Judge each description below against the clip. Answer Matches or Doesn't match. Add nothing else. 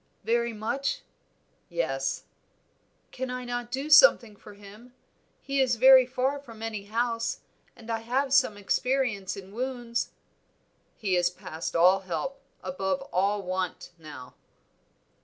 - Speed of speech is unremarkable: Doesn't match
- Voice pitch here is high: Matches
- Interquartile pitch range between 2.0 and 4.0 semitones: Doesn't match